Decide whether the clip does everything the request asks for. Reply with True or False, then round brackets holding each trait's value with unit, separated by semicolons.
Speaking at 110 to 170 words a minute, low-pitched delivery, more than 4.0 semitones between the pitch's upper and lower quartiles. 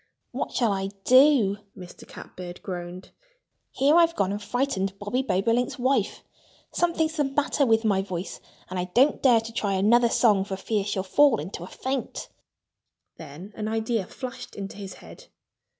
False (165 wpm; 220 Hz; 5.1 semitones)